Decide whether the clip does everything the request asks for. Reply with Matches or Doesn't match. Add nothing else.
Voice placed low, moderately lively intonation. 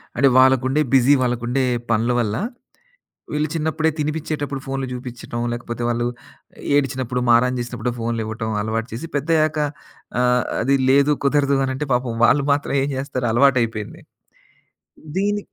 Matches